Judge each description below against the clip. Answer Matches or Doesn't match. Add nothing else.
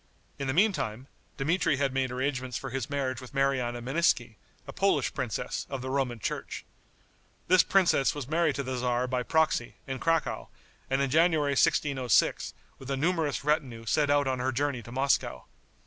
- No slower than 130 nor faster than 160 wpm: Doesn't match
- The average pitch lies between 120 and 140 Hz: Matches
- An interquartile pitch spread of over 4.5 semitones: Doesn't match